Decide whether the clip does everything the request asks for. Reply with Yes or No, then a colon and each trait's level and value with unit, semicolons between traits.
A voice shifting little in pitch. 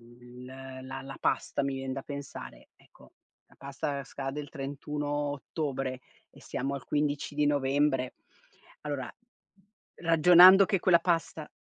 Yes: narrow, 1.9 semitones